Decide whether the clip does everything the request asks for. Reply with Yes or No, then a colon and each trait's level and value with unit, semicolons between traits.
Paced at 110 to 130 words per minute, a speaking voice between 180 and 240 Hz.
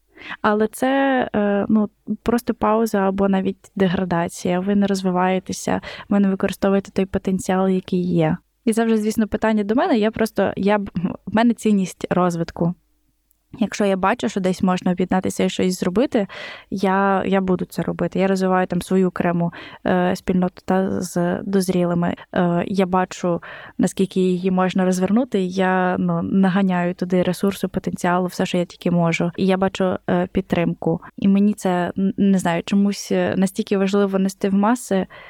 No: average, 150 wpm; high, 190 Hz